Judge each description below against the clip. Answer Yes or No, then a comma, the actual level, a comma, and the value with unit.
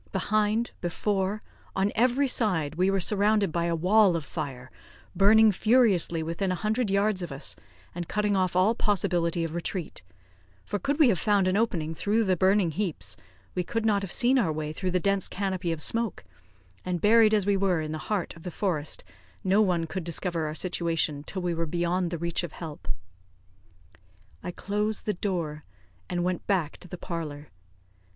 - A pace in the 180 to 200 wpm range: Yes, average, 185 wpm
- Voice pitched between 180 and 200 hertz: Yes, medium, 185 Hz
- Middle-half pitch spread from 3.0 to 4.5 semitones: Yes, average, 3.8 semitones